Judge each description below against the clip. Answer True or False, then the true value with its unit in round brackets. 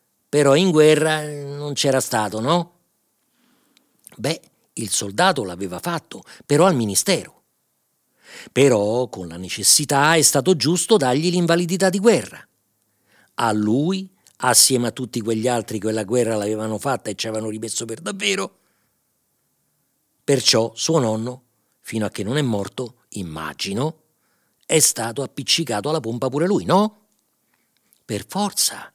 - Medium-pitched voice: False (130 Hz)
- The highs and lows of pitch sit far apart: True (6.3 semitones)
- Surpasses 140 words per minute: False (135 wpm)